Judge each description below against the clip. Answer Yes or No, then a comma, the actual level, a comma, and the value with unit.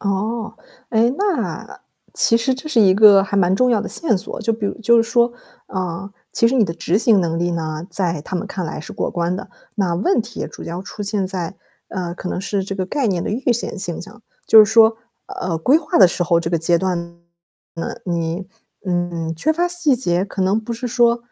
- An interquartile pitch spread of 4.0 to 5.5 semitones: Yes, average, 4.7 semitones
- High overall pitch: Yes, high, 195 Hz